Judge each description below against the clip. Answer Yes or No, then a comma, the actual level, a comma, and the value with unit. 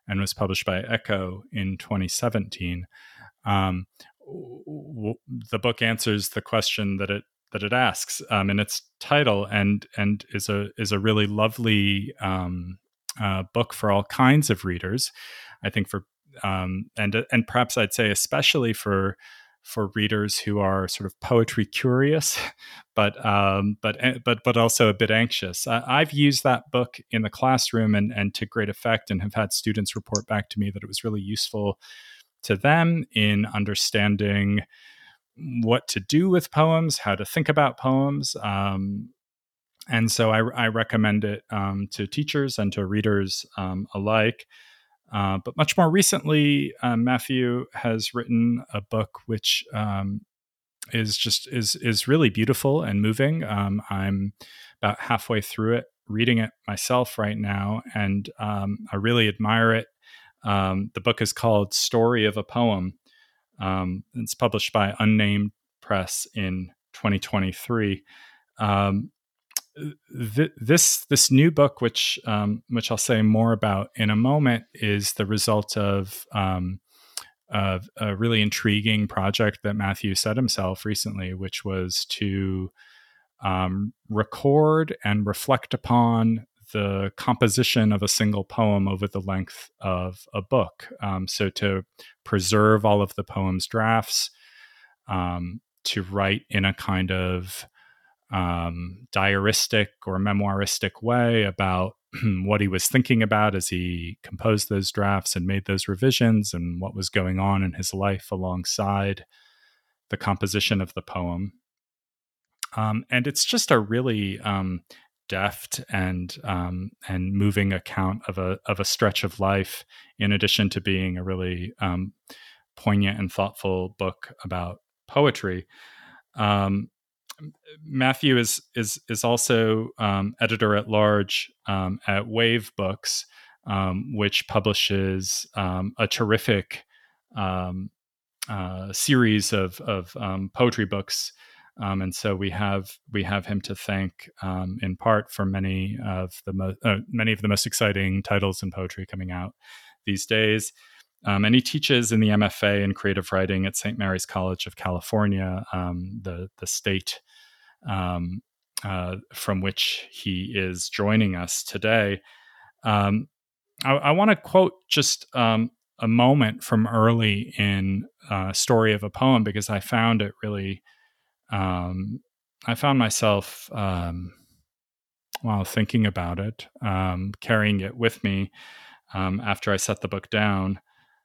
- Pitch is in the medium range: No, low, 105 Hz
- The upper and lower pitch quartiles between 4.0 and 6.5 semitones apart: No, average, 2.9 semitones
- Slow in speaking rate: No, average, 145 wpm